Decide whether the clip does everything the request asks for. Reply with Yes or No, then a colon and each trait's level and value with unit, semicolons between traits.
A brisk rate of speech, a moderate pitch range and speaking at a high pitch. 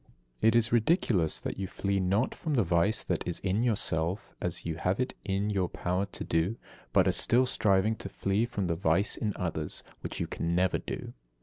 No: fast, 210 wpm; average, 3.8 semitones; low, 100 Hz